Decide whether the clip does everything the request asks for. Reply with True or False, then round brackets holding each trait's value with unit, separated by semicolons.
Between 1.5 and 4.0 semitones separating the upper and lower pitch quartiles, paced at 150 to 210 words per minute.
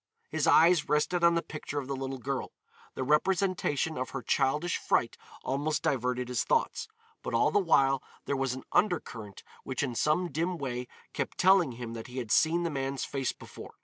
False (4.4 semitones; 190 wpm)